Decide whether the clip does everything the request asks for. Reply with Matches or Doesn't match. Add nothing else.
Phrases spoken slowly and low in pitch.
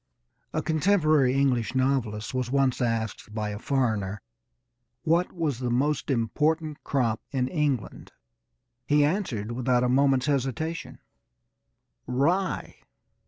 Matches